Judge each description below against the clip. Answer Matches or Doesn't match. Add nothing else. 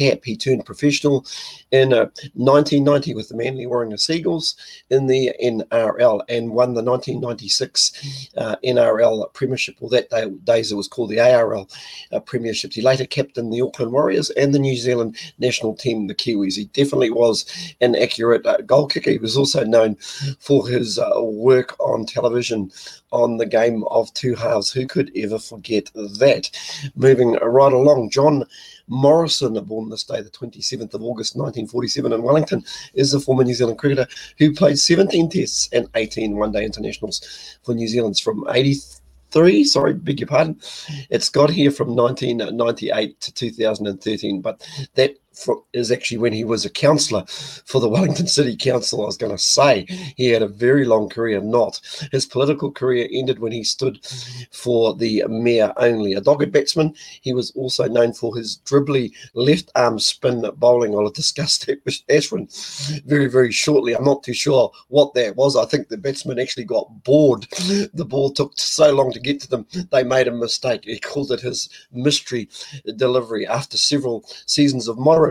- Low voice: Matches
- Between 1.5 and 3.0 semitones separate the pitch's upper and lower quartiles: Doesn't match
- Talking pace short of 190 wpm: Matches